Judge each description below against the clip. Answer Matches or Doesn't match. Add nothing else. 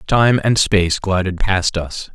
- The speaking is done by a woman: Doesn't match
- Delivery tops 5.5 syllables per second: Doesn't match